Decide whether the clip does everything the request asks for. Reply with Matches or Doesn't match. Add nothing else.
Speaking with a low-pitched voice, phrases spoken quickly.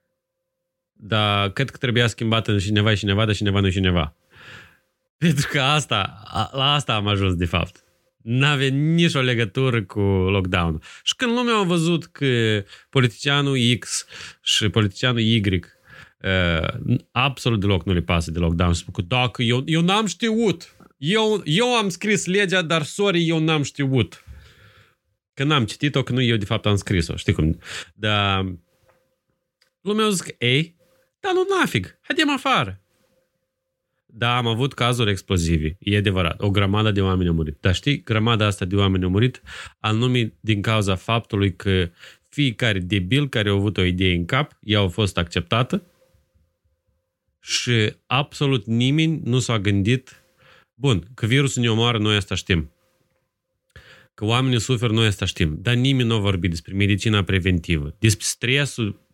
Doesn't match